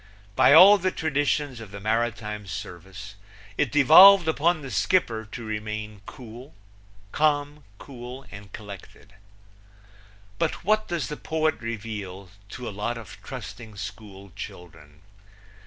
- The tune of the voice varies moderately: No, wide, 6.3 semitones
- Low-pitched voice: Yes, low, 115 Hz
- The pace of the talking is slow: Yes, slow, 125 wpm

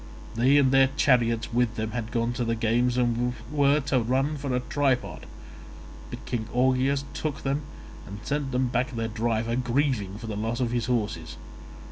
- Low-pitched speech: Yes, low, 125 Hz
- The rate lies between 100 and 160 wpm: No, average, 175 wpm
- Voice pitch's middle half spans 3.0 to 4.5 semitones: No, narrow, 2.6 semitones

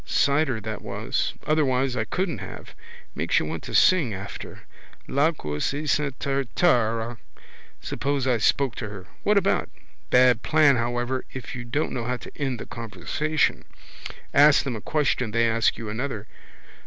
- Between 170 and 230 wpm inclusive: No, average, 155 wpm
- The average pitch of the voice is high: No, low, 125 Hz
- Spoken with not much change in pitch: No, average, 3.9 semitones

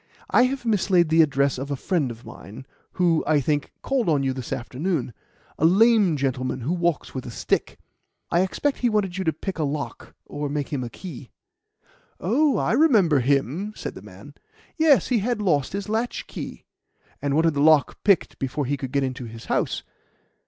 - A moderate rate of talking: Yes, average, 190 wpm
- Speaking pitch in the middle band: Yes, medium, 155 Hz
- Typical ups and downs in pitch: No, wide, 6.5 semitones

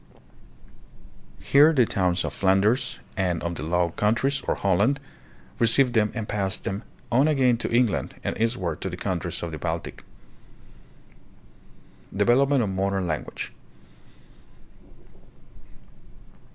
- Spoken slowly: Yes, slow, 120 wpm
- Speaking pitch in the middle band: No, low, 105 Hz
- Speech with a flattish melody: No, average, 5.0 semitones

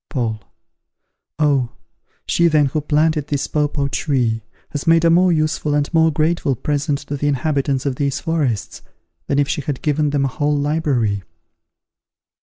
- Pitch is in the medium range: Yes, medium, 145 Hz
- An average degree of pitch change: No, narrow, 2.0 semitones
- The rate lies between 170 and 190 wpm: No, average, 160 wpm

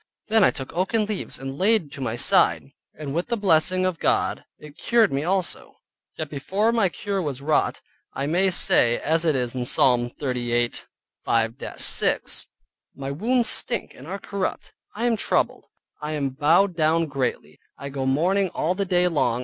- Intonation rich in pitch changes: Yes, wide, 6.2 semitones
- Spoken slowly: No, average, 175 wpm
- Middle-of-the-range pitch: Yes, medium, 160 Hz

